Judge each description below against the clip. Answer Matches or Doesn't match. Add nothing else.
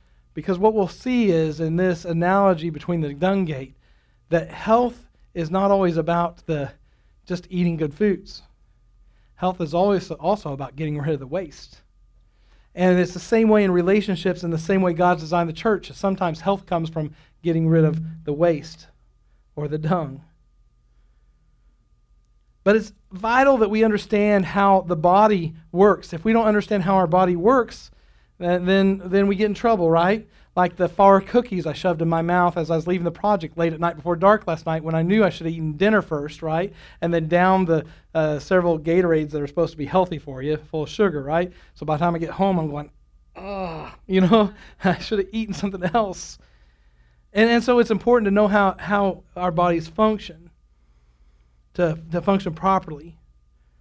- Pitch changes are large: Doesn't match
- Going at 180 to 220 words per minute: Matches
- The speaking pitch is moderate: Matches